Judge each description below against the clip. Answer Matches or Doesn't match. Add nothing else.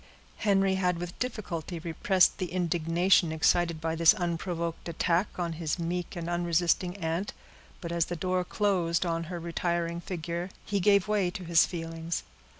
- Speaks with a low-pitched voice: Doesn't match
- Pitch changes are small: Matches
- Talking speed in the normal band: Matches